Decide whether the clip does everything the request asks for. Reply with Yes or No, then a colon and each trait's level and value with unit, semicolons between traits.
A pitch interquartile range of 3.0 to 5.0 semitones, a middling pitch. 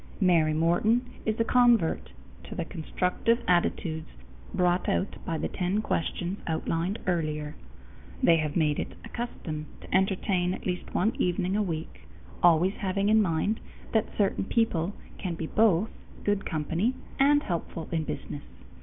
Yes: average, 4.1 semitones; medium, 180 Hz